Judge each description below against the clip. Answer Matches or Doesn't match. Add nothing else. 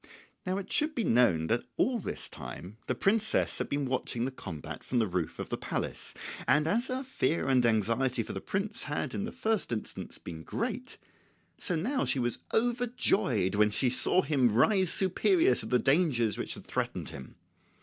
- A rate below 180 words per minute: Doesn't match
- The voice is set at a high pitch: Doesn't match